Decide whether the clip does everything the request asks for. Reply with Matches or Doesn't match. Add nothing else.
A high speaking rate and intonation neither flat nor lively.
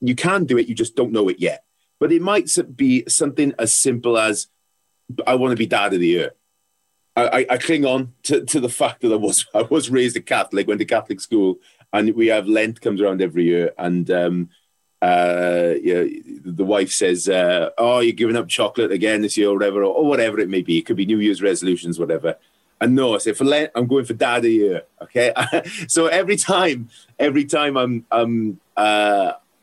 Doesn't match